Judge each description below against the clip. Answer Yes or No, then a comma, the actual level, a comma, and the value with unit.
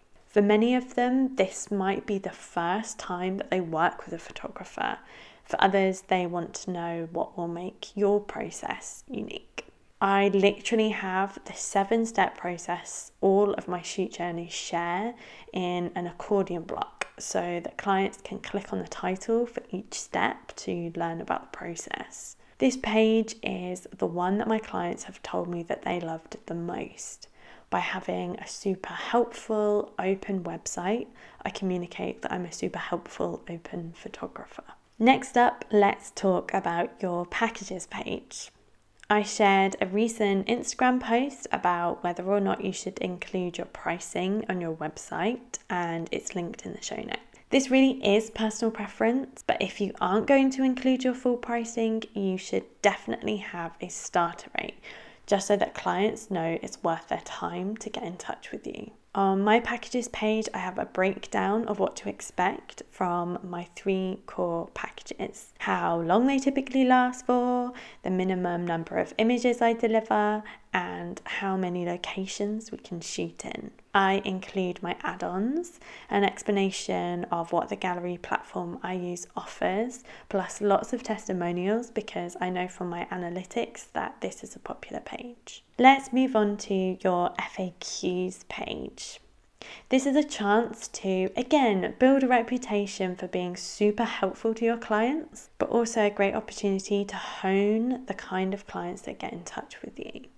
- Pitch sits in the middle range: No, high, 200 Hz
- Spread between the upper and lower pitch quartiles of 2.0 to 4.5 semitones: Yes, average, 3.8 semitones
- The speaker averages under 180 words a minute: Yes, average, 165 wpm